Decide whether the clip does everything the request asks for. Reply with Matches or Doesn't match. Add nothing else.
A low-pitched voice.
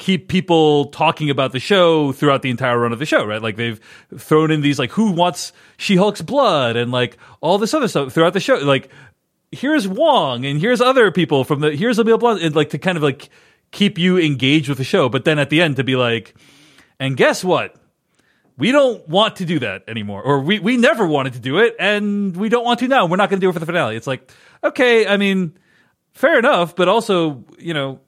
Doesn't match